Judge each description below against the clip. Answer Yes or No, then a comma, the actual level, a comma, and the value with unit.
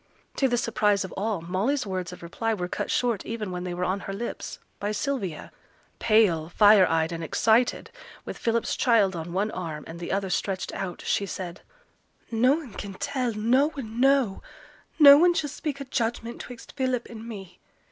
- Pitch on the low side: No, high, 215 Hz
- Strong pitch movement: No, average, 4.8 semitones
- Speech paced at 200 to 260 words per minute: No, average, 180 wpm